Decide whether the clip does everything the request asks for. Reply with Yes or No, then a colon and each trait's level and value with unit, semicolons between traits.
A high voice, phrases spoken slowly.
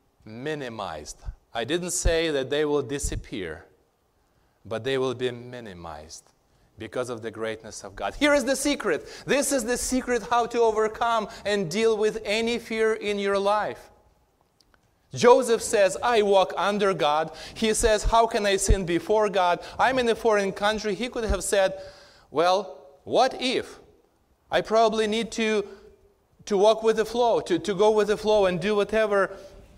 No: high, 205 Hz; average, 165 wpm